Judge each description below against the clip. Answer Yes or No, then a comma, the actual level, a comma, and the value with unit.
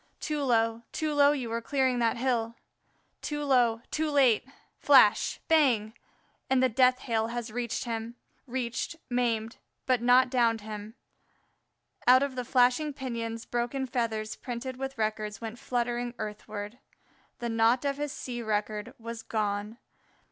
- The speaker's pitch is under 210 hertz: No, high, 240 Hz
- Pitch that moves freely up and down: No, narrow, 2.5 semitones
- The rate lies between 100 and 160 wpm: Yes, average, 145 wpm